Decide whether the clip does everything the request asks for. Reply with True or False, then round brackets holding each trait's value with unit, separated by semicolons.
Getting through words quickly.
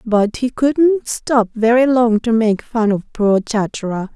False (175 wpm)